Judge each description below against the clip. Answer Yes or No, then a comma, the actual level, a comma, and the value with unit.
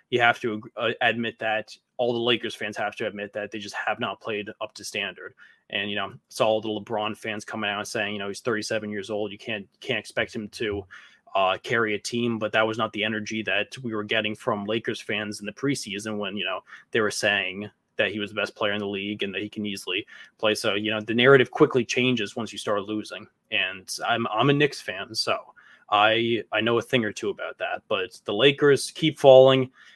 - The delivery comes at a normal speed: No, fast, 235 wpm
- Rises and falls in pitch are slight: Yes, narrow, 2.3 semitones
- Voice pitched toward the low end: Yes, low, 110 Hz